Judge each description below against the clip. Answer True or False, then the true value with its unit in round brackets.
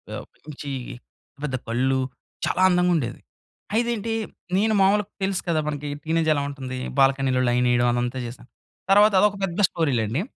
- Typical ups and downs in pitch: False (6.9 semitones)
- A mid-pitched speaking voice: True (145 Hz)